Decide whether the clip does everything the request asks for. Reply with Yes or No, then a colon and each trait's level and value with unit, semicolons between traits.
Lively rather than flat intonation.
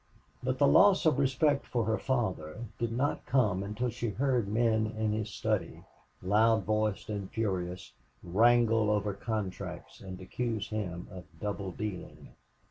No: average, 3.4 semitones